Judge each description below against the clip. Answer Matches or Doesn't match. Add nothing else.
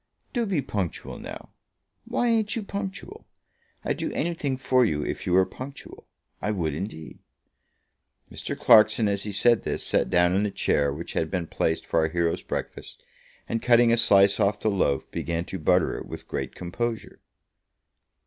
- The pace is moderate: Matches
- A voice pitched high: Doesn't match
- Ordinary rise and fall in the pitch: Doesn't match